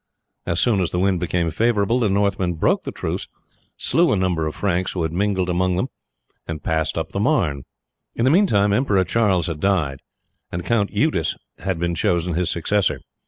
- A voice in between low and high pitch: No, very low, 95 Hz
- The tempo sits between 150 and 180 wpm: No, average, 190 wpm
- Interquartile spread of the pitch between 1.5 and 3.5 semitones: Yes, average, 3.2 semitones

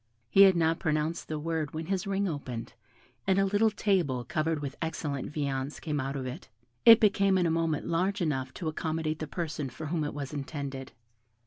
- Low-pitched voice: No, medium, 155 Hz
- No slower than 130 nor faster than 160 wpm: No, average, 200 wpm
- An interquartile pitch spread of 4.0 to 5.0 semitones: No, average, 3.6 semitones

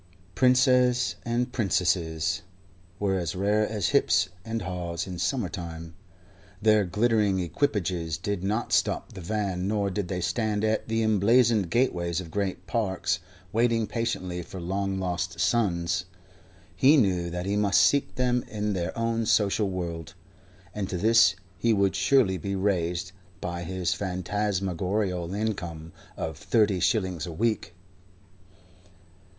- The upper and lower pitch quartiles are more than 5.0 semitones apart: No, average, 3.6 semitones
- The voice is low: Yes, very low, 95 Hz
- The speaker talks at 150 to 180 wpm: No, slow, 135 wpm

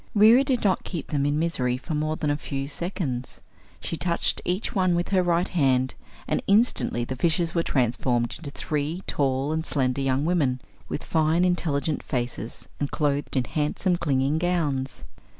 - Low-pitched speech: No, medium, 150 Hz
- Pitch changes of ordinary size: Yes, average, 4.4 semitones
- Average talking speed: Yes, average, 170 wpm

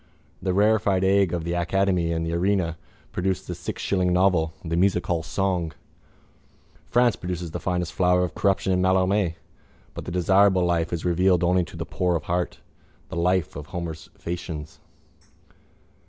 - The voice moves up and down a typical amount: No, narrow, 1.9 semitones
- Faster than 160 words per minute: No, average, 155 wpm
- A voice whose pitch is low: Yes, very low, 90 Hz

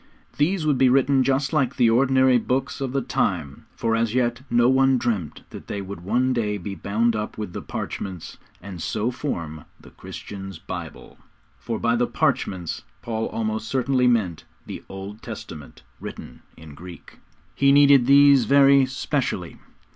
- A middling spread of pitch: Yes, average, 5.0 semitones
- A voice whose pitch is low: Yes, low, 120 Hz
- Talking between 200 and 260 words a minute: No, average, 160 wpm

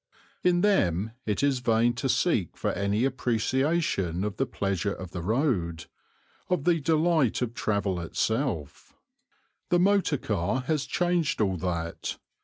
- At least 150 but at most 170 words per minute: No, average, 140 wpm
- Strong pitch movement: Yes, wide, 8.2 semitones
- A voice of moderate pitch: No, low, 115 Hz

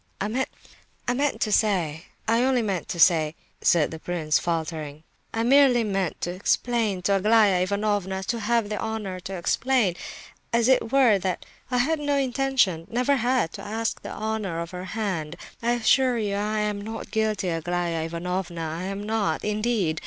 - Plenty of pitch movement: No, average, 4.7 semitones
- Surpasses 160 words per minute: No, average, 155 wpm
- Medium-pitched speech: No, high, 205 Hz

